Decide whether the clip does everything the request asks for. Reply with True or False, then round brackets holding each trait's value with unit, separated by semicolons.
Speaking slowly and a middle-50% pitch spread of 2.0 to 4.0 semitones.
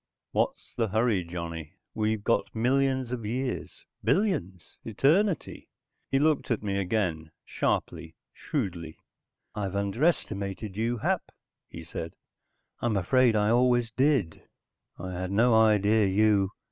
False (120 wpm; 4.6 semitones)